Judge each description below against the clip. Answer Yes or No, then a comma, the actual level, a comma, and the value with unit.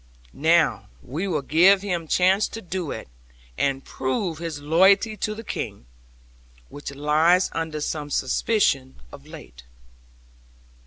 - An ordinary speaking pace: No, slow, 125 wpm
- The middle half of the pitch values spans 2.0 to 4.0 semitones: No, average, 4.6 semitones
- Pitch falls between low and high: Yes, medium, 165 Hz